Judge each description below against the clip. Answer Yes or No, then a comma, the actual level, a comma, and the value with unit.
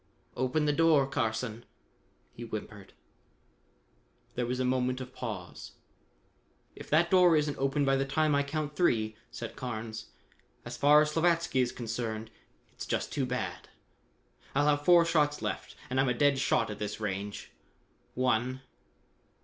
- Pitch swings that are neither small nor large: Yes, average, 4.4 semitones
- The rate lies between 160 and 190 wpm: No, average, 150 wpm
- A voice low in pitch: Yes, low, 130 Hz